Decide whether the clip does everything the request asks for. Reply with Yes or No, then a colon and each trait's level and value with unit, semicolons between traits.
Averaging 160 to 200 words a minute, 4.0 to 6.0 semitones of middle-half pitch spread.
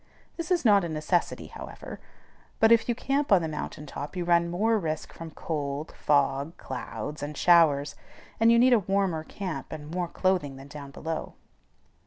Yes: average, 180 wpm; average, 5.1 semitones